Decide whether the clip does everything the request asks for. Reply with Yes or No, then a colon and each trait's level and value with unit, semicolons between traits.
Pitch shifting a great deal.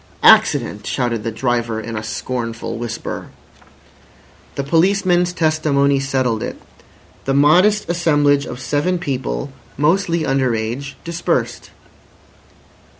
Yes: wide, 5.8 semitones